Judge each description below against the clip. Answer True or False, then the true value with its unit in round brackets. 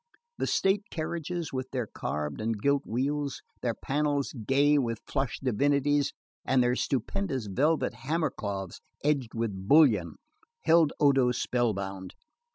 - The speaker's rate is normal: False (130 wpm)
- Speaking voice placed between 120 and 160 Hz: True (135 Hz)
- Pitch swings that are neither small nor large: True (4.4 semitones)